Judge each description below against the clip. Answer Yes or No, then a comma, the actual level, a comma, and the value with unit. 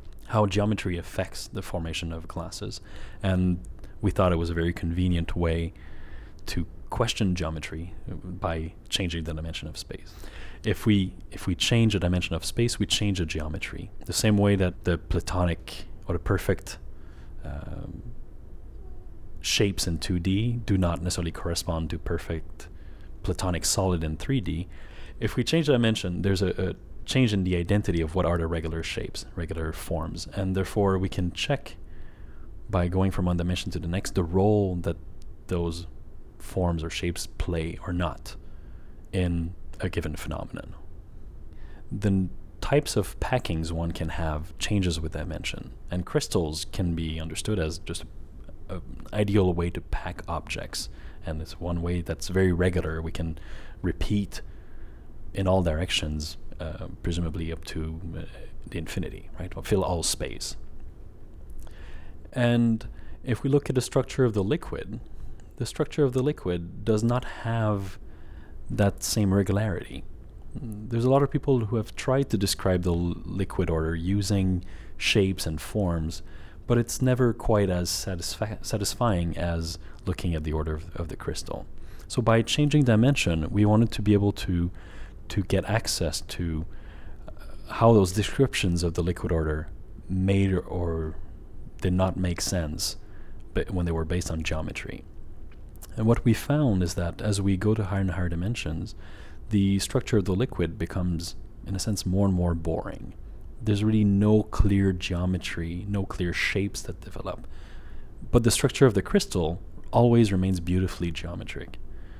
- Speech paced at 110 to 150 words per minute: No, average, 160 wpm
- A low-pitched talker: Yes, very low, 90 Hz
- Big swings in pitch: No, average, 3.5 semitones